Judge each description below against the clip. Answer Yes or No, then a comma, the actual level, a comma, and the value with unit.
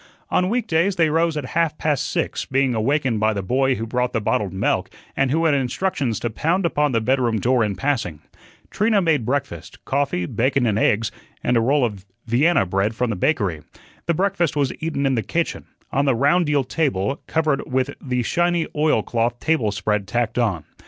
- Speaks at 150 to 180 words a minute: No, average, 195 wpm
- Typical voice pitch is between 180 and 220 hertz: No, low, 130 Hz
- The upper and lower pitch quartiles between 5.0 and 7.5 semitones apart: Yes, wide, 5.5 semitones